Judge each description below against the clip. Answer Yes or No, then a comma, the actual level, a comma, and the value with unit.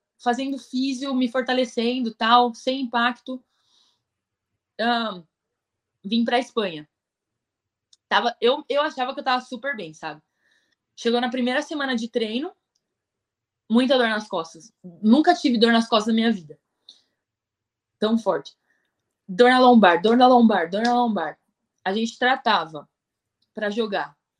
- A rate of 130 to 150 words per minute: Yes, average, 140 wpm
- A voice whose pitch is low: No, high, 230 Hz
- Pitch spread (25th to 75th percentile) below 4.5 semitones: No, average, 5.2 semitones